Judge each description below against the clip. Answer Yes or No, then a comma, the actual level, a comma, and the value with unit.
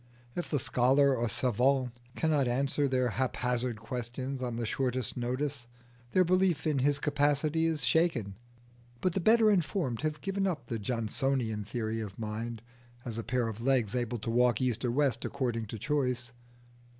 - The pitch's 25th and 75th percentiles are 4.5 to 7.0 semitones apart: No, average, 3.7 semitones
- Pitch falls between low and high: No, low, 125 Hz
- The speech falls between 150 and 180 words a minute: Yes, average, 165 wpm